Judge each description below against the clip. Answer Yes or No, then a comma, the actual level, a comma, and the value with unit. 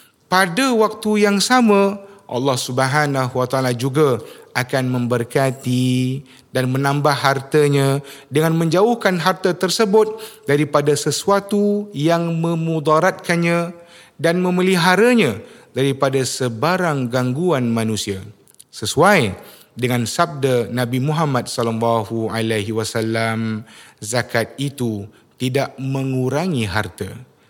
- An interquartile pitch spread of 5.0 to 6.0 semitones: Yes, wide, 5.6 semitones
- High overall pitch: No, medium, 140 Hz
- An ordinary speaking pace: No, slow, 90 wpm